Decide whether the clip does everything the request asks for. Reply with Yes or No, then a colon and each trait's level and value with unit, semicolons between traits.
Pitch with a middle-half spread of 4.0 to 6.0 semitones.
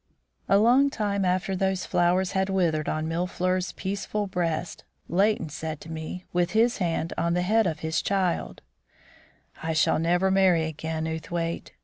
No: average, 2.8 semitones